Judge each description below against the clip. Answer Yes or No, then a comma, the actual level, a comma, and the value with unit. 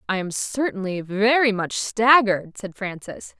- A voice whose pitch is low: No, high, 210 Hz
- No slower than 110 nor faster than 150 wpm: Yes, average, 140 wpm